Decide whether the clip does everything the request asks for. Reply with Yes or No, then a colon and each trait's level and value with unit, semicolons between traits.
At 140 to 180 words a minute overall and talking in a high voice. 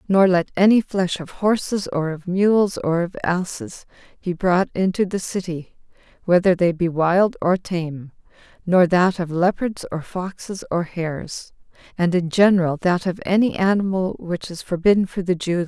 No: average, 175 wpm; medium, 180 Hz